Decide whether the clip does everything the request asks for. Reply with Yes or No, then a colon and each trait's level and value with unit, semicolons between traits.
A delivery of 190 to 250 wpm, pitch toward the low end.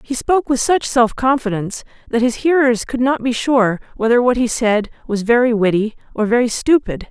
No: average, 195 wpm; high, 240 Hz